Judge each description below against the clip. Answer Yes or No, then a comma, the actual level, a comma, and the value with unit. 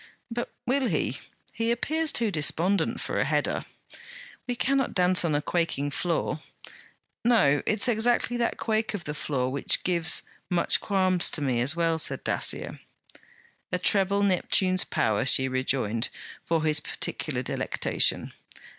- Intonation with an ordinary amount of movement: No, wide, 6.9 semitones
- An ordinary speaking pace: Yes, average, 145 wpm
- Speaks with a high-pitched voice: No, medium, 180 Hz